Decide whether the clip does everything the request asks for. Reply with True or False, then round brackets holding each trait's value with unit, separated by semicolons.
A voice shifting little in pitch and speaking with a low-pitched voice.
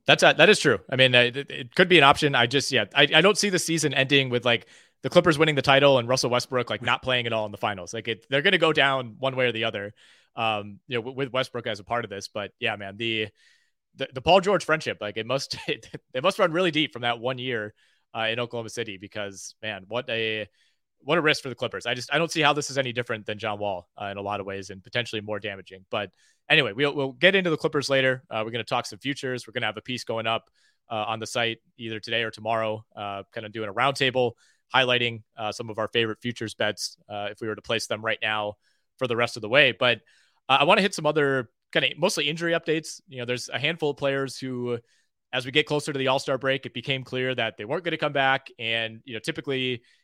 False (3.8 semitones; 125 Hz)